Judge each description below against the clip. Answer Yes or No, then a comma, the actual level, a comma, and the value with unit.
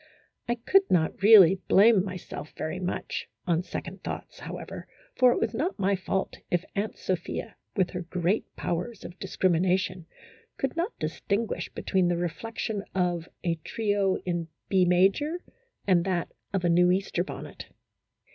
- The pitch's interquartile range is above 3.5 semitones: No, average, 2.7 semitones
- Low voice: No, medium, 185 Hz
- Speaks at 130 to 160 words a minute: Yes, average, 155 wpm